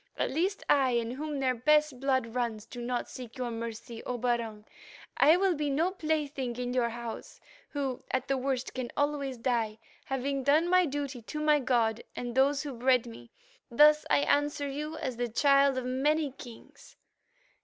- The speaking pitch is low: No, very high, 260 Hz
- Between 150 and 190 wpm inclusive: Yes, average, 175 wpm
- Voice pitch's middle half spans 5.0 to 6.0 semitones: No, average, 3.3 semitones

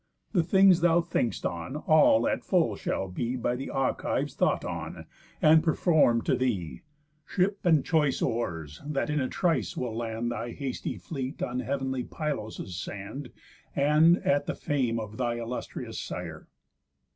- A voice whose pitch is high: No, low, 130 Hz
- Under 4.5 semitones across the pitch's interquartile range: No, average, 4.9 semitones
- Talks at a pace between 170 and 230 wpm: No, average, 155 wpm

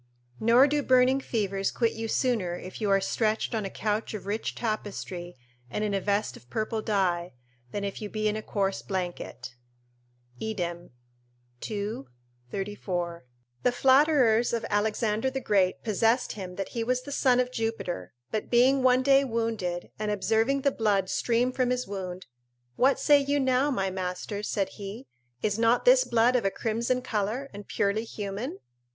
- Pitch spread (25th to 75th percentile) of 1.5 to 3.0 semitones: No, average, 4.2 semitones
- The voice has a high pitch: Yes, high, 215 Hz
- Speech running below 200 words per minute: Yes, average, 170 wpm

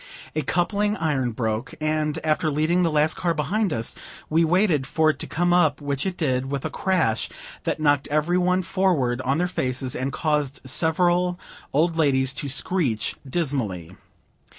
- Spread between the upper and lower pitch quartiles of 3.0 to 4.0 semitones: No, average, 4.8 semitones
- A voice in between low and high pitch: Yes, medium, 155 Hz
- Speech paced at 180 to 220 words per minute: No, average, 170 wpm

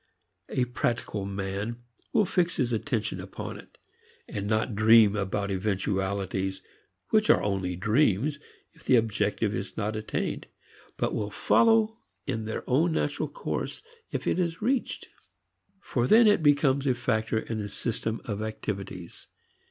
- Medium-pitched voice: No, low, 110 Hz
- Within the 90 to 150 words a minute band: Yes, average, 145 wpm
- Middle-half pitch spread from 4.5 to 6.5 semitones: Yes, wide, 5.6 semitones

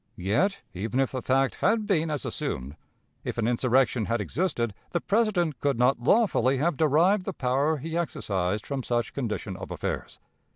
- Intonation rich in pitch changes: Yes, wide, 6.3 semitones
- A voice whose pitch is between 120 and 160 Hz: Yes, low, 135 Hz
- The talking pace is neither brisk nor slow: Yes, average, 170 wpm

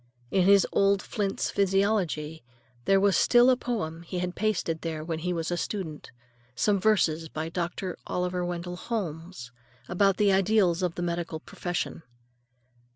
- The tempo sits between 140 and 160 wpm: Yes, average, 155 wpm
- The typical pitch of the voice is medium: Yes, medium, 180 Hz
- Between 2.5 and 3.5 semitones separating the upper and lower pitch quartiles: Yes, average, 3.1 semitones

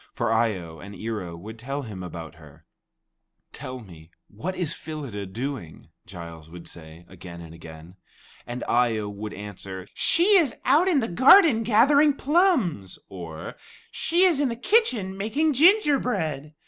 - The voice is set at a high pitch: No, low, 120 Hz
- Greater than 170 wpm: No, average, 160 wpm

